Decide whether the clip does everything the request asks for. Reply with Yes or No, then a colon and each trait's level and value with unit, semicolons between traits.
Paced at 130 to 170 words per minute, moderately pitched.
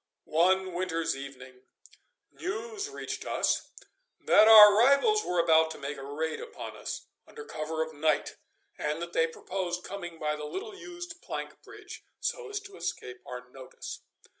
Yes: average, 160 wpm; medium, 175 Hz